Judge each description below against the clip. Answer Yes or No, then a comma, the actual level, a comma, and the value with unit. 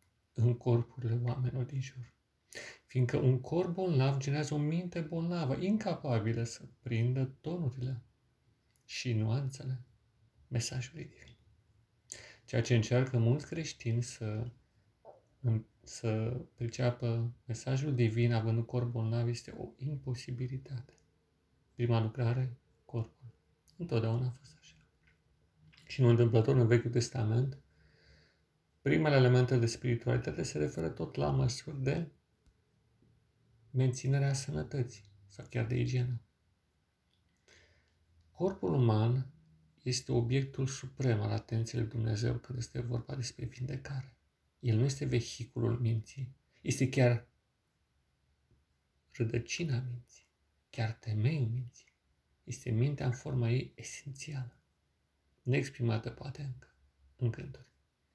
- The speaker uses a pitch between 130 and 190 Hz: No, low, 120 Hz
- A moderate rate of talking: No, slow, 105 wpm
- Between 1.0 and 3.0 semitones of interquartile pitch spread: Yes, narrow, 2.6 semitones